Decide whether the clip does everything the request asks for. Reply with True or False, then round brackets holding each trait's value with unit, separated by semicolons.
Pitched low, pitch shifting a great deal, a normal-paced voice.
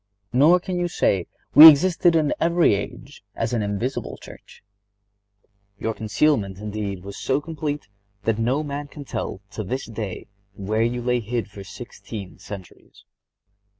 True (120 Hz; 6.3 semitones; 150 wpm)